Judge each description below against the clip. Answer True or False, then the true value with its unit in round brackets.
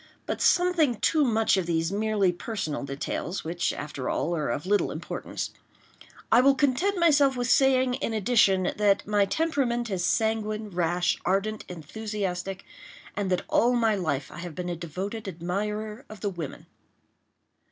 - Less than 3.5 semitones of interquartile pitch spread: False (5.0 semitones)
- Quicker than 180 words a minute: False (150 wpm)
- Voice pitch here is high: True (205 Hz)